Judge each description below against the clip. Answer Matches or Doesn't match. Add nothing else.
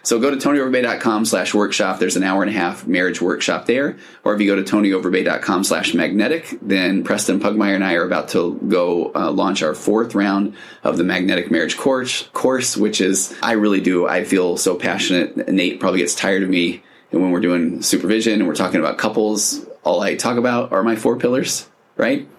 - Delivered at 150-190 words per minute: Doesn't match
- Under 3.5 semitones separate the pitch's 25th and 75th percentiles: Matches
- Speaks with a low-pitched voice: Matches